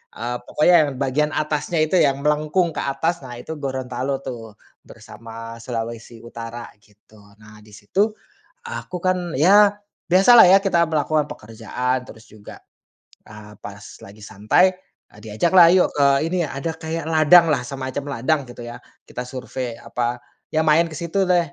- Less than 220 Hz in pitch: Yes, medium, 140 Hz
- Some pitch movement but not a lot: No, wide, 6.0 semitones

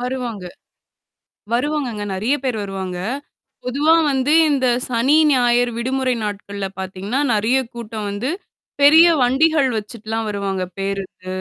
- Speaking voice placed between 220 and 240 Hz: Yes, high, 235 Hz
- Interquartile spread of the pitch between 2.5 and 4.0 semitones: No, average, 4.6 semitones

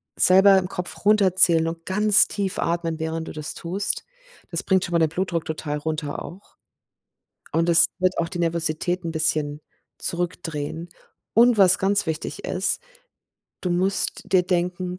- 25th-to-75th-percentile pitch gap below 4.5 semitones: Yes, narrow, 2.5 semitones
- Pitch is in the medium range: Yes, medium, 175 Hz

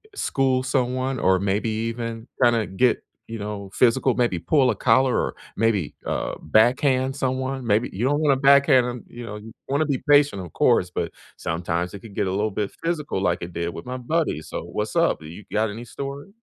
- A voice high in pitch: No, low, 120 Hz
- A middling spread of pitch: Yes, average, 4.5 semitones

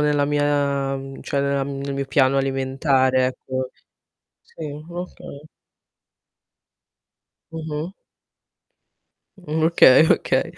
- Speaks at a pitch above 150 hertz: No, medium, 140 Hz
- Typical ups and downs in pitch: No, narrow, 1.8 semitones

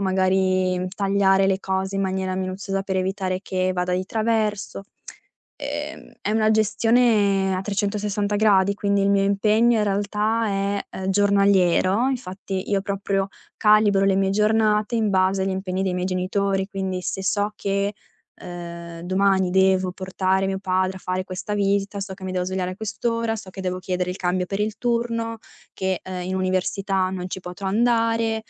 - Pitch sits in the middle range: No, high, 195 Hz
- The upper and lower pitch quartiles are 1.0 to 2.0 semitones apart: Yes, narrow, 1.7 semitones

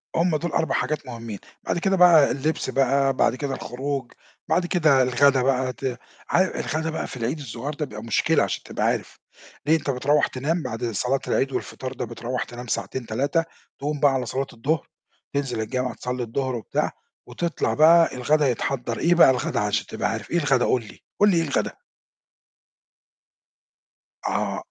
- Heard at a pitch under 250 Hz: Yes, low, 135 Hz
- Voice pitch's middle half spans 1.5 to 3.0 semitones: No, average, 3.7 semitones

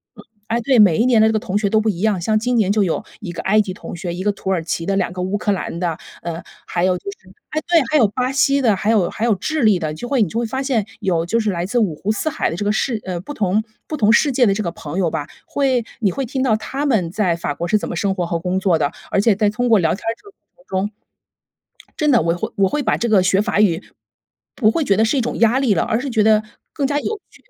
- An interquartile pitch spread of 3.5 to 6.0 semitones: Yes, average, 4.5 semitones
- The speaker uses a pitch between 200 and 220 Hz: Yes, high, 210 Hz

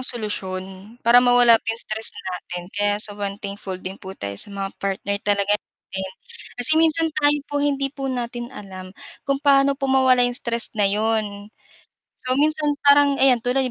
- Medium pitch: No, high, 235 Hz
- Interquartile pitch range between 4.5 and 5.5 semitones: Yes, average, 5.2 semitones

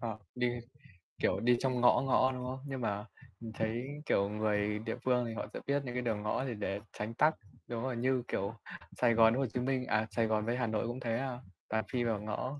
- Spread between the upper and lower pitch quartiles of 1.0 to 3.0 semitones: Yes, narrow, 2.6 semitones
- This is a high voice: No, low, 120 Hz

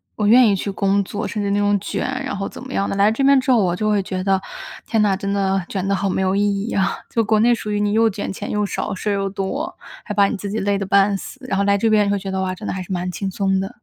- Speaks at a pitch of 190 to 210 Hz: Yes, high, 200 Hz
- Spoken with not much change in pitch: Yes, narrow, 1.6 semitones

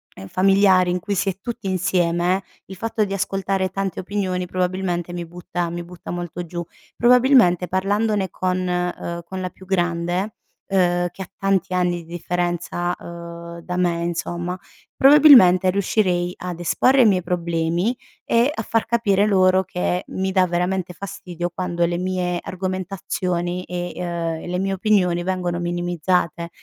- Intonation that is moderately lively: No, narrow, 1.8 semitones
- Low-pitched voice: No, medium, 180 Hz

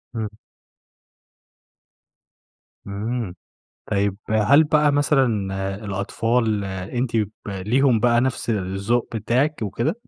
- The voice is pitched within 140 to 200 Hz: No, low, 115 Hz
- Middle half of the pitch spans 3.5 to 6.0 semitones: Yes, average, 3.9 semitones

